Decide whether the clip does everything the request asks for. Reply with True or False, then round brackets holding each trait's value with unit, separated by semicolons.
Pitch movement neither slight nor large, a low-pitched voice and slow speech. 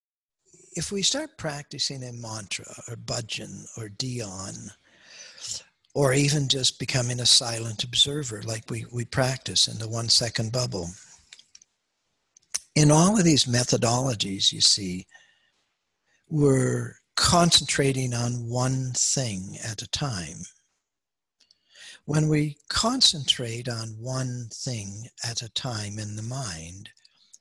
True (3.7 semitones; 125 Hz; 115 wpm)